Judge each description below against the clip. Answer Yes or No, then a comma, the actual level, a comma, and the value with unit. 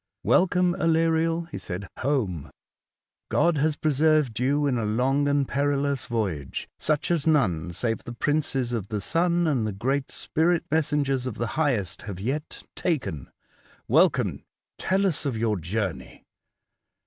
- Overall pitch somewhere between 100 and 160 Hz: Yes, medium, 140 Hz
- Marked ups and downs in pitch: Yes, wide, 5.9 semitones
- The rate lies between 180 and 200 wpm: No, average, 145 wpm